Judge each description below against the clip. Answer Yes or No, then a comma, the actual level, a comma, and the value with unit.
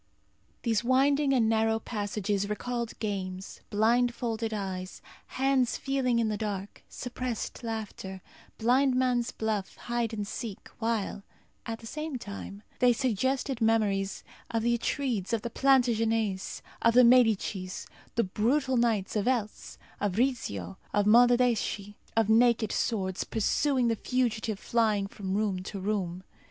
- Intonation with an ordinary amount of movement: Yes, average, 3.2 semitones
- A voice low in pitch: No, high, 225 Hz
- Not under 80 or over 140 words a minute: Yes, slow, 135 wpm